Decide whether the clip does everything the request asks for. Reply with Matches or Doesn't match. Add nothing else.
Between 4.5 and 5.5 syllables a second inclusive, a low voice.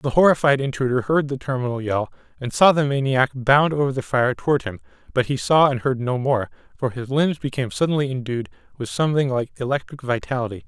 Doesn't match